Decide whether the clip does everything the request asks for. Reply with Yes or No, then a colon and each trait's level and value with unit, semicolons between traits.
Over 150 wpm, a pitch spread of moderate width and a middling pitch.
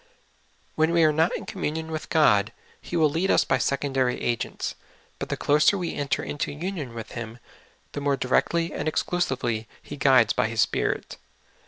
Yes: average, 180 wpm; average, 4.5 semitones; medium, 145 Hz